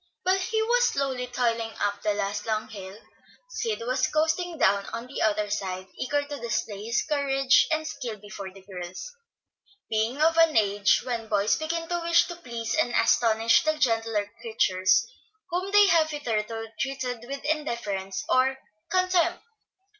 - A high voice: Yes, high, 240 Hz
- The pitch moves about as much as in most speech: No, wide, 6.7 semitones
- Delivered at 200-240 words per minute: No, average, 160 wpm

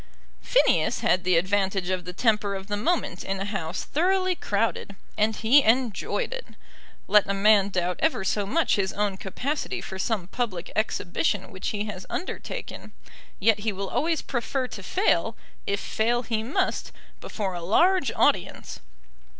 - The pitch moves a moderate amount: Yes, average, 4.3 semitones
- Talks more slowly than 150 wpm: No, average, 160 wpm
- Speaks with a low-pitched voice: No, high, 210 Hz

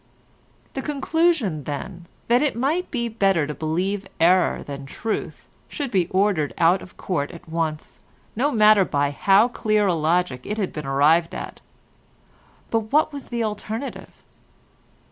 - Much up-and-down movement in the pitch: Yes, wide, 6.2 semitones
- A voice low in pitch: No, high, 195 Hz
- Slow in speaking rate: No, average, 150 wpm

